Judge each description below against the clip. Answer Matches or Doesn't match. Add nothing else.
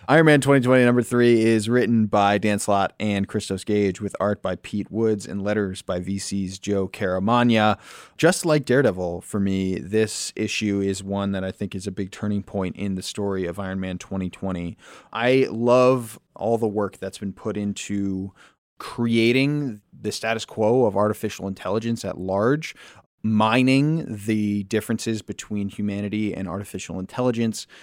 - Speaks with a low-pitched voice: Matches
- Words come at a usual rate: Matches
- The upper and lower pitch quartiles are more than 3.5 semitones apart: Doesn't match